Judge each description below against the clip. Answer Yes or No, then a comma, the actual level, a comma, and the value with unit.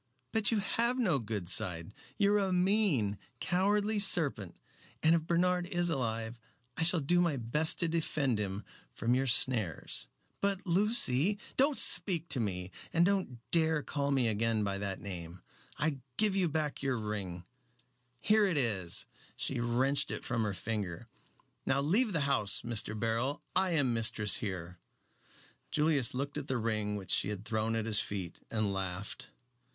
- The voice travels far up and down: Yes, wide, 8.6 semitones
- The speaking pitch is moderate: No, low, 130 Hz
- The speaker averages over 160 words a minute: Yes, average, 170 wpm